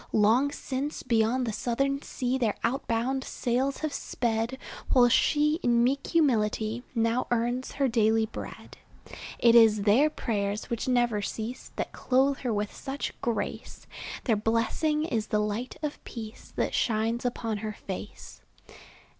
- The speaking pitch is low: No, high, 235 Hz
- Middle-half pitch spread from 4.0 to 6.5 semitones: No, average, 3.1 semitones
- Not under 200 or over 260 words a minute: No, average, 145 wpm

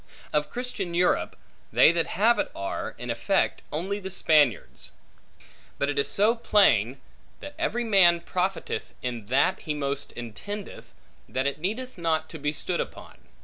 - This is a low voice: No, medium, 170 Hz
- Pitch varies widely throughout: Yes, wide, 6.3 semitones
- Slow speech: No, average, 155 wpm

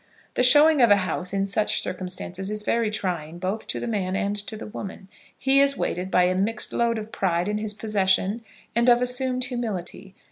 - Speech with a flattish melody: No, average, 3.8 semitones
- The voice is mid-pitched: No, high, 210 Hz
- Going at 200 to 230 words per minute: Yes, fast, 205 wpm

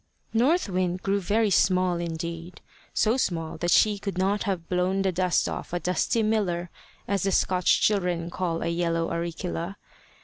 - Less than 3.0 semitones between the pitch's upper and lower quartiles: Yes, narrow, 2.6 semitones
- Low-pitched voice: No, medium, 180 Hz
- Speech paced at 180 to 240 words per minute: No, average, 165 wpm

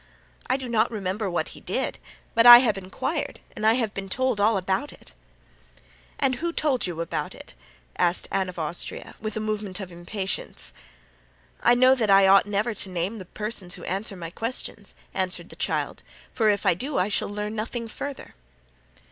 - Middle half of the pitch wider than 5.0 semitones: No, average, 3.6 semitones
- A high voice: Yes, high, 210 Hz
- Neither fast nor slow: Yes, average, 190 wpm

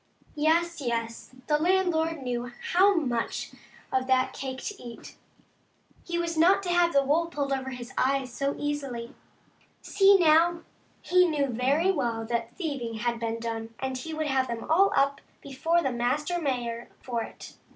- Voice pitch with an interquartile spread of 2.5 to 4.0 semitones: No, wide, 5.6 semitones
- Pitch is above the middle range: Yes, very high, 275 Hz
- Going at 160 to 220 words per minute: Yes, average, 165 wpm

